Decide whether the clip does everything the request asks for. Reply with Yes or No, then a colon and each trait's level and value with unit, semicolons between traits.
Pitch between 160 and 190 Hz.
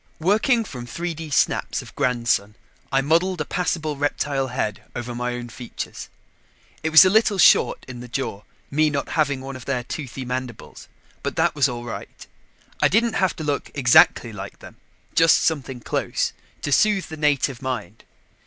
No: medium, 140 Hz